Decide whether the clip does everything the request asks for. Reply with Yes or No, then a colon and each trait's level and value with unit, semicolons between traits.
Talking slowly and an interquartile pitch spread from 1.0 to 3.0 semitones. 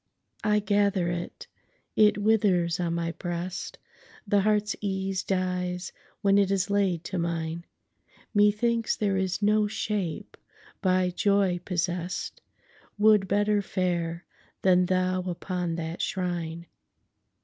Yes: slow, 105 wpm; average, 2.7 semitones